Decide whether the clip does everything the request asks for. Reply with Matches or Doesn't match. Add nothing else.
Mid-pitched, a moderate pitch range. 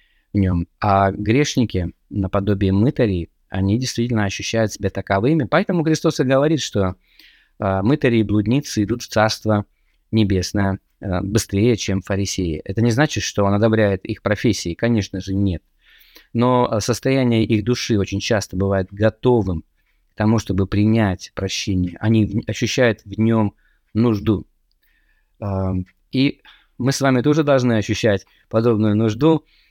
Doesn't match